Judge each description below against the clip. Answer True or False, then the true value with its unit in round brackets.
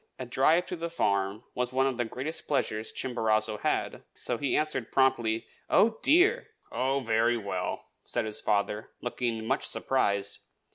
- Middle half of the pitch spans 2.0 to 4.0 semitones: True (3.7 semitones)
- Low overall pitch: True (120 Hz)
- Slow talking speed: False (155 wpm)